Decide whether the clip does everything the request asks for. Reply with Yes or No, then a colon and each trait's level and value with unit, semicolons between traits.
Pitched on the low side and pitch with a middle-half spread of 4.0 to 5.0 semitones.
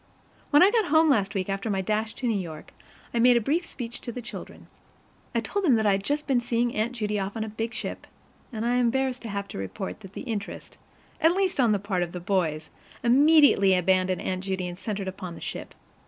No: high, 220 Hz; average, 4.5 semitones